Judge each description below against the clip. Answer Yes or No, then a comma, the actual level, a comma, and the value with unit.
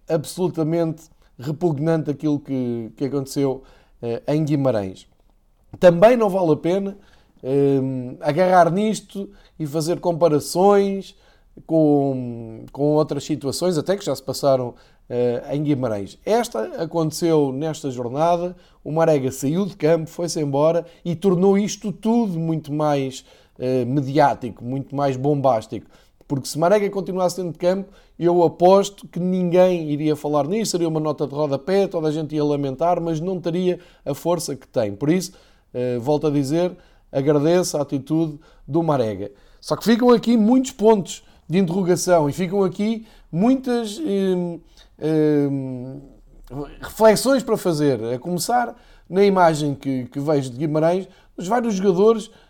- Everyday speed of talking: Yes, average, 145 wpm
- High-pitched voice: No, medium, 160 Hz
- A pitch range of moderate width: Yes, average, 4.6 semitones